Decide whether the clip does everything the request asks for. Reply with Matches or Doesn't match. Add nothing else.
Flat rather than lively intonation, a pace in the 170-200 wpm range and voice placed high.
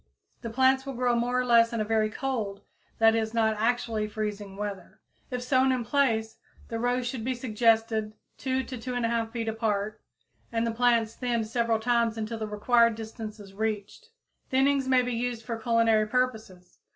Matches